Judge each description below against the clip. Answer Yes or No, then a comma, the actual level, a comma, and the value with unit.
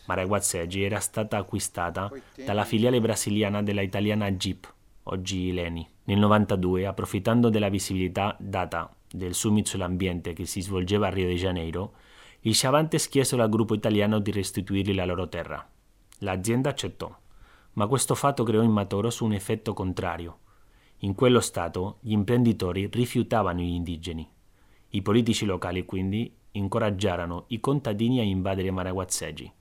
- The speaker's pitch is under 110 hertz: Yes, low, 100 Hz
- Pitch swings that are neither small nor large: Yes, average, 3.1 semitones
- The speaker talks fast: No, average, 140 wpm